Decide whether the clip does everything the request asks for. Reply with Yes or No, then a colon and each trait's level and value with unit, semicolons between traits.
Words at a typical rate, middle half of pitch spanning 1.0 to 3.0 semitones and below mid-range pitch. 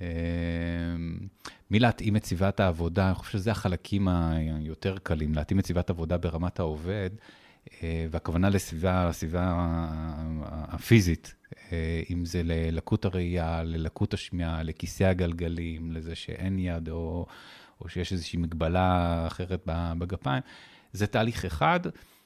Yes: average, 110 wpm; narrow, 2.4 semitones; very low, 85 Hz